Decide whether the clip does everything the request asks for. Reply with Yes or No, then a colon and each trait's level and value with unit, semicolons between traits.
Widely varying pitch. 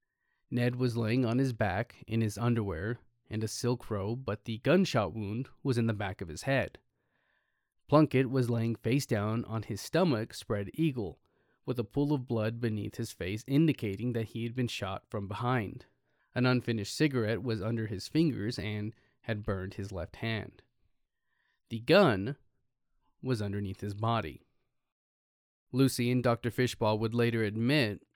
No: average, 3.1 semitones